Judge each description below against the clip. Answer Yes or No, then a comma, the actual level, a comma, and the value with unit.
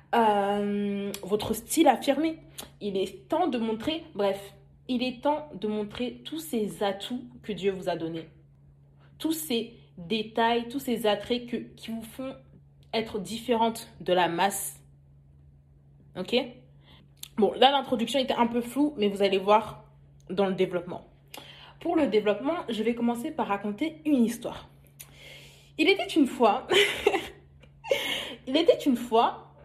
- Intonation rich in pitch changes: Yes, wide, 5.9 semitones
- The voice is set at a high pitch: Yes, high, 220 Hz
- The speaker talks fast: No, slow, 145 wpm